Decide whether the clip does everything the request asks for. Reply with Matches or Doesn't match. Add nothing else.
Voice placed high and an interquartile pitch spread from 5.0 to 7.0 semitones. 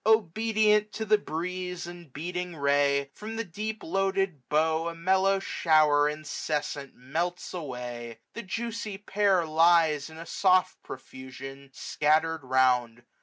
Doesn't match